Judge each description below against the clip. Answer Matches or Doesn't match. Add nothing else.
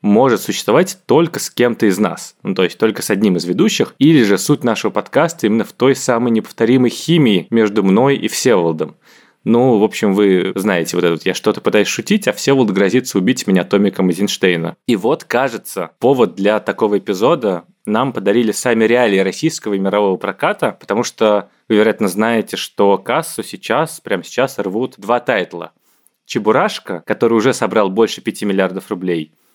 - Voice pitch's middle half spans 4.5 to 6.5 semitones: Doesn't match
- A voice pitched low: Matches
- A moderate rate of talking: Doesn't match